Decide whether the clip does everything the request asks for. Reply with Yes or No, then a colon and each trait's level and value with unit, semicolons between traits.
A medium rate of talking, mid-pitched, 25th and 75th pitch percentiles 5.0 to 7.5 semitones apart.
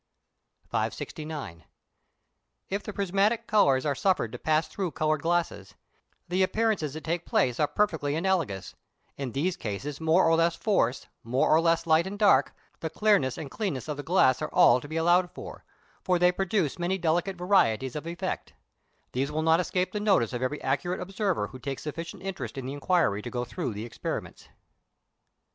Yes: average, 180 wpm; medium, 160 Hz; average, 5.3 semitones